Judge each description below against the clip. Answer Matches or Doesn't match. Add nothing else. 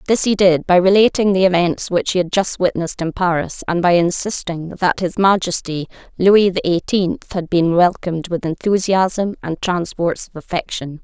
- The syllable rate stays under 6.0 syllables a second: Matches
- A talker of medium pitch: Matches